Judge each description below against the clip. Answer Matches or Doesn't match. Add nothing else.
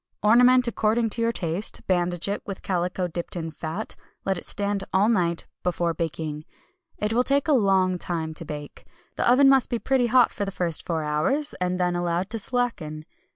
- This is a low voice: Doesn't match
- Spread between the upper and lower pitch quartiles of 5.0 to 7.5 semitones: Matches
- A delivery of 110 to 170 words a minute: Doesn't match